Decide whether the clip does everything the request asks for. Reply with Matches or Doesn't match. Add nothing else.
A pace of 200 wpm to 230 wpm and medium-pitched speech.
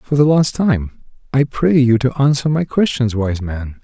Doesn't match